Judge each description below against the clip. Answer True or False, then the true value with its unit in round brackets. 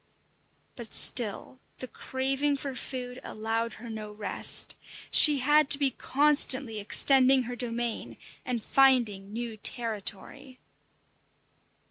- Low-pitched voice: False (250 Hz)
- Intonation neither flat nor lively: True (3.2 semitones)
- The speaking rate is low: True (110 wpm)